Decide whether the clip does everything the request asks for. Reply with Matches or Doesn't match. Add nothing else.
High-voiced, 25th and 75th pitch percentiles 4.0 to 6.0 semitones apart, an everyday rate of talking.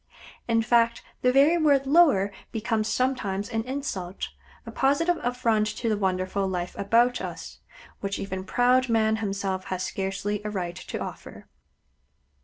Matches